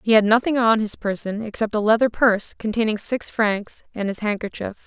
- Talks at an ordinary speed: Yes, average, 195 wpm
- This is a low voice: No, high, 215 Hz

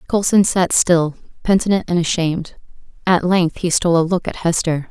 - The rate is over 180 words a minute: No, average, 170 wpm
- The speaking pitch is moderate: Yes, medium, 175 Hz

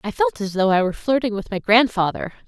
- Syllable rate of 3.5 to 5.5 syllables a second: No, 6.2 syllables/s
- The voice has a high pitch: Yes, high, 220 Hz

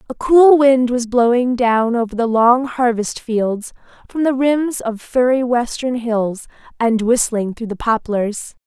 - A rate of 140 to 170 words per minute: Yes, average, 160 wpm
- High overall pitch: Yes, high, 240 Hz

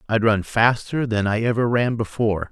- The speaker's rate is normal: Yes, average, 190 wpm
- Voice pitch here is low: Yes, low, 110 Hz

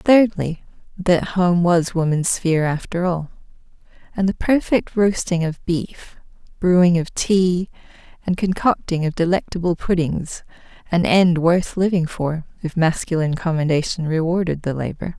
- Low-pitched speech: No, medium, 175 Hz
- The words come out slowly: Yes, slow, 130 wpm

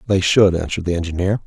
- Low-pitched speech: Yes, very low, 90 Hz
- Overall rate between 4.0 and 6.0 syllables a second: No, 7.1 syllables/s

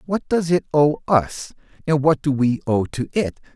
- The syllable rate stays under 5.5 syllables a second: Yes, 4.3 syllables/s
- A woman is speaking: No, male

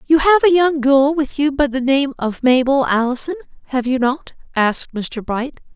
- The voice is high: Yes, very high, 275 Hz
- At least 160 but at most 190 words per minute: No, average, 200 wpm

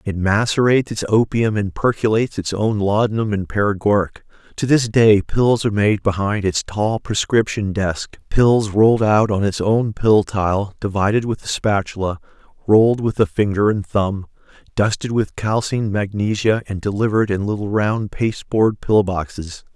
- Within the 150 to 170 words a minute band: Yes, average, 155 wpm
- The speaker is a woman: No, male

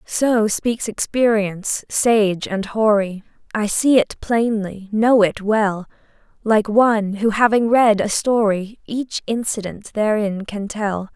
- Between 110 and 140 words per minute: Yes, slow, 135 wpm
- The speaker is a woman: Yes, female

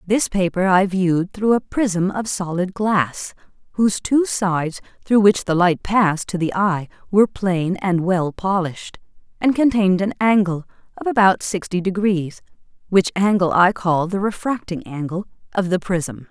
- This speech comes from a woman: Yes, female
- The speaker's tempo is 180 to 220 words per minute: No, average, 160 wpm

